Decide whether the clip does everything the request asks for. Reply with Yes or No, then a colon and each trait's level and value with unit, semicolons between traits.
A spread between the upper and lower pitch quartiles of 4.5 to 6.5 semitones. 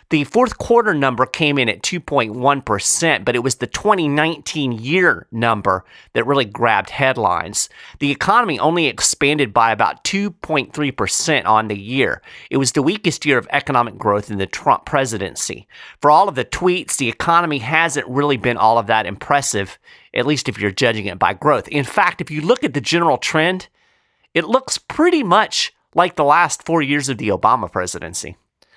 Yes: average, 5.2 semitones